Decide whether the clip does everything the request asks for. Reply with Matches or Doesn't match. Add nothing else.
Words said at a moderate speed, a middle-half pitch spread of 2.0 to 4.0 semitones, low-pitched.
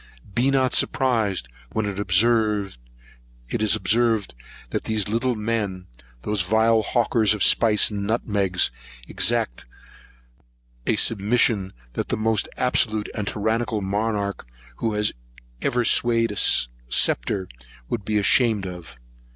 Doesn't match